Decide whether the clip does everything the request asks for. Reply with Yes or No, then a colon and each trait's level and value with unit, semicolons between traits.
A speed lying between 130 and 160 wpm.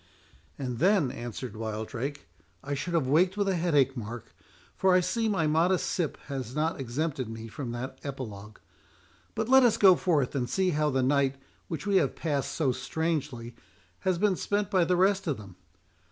No: average, 180 wpm